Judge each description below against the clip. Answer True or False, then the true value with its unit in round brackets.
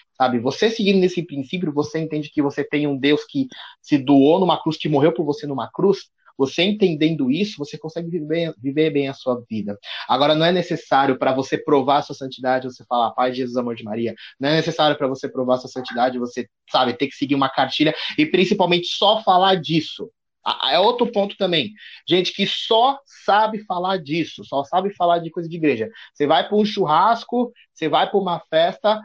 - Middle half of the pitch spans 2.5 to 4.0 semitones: False (5.1 semitones)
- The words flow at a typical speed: False (200 wpm)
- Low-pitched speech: False (155 Hz)